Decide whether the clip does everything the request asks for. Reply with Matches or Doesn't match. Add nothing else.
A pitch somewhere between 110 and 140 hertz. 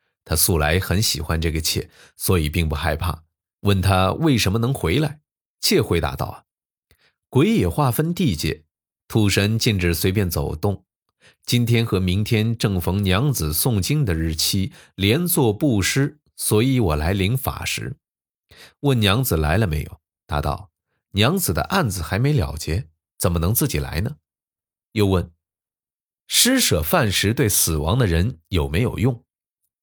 Doesn't match